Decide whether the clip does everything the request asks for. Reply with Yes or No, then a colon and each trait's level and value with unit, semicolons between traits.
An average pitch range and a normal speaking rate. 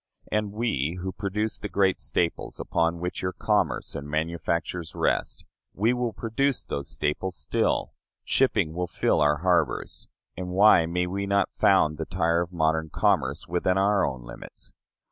Yes: average, 3.8 semitones; average, 160 wpm